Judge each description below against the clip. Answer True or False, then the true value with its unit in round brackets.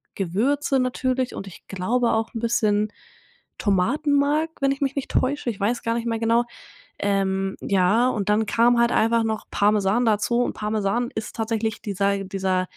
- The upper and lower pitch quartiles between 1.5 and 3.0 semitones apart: False (3.4 semitones)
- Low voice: False (225 Hz)